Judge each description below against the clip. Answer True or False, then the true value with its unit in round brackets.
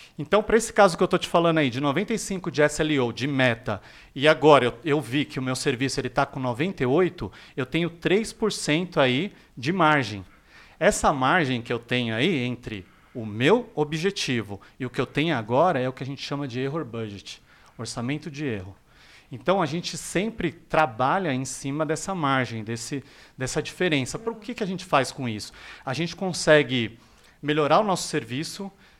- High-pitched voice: False (145 Hz)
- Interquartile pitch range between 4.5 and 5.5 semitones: True (5.1 semitones)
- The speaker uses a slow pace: False (185 wpm)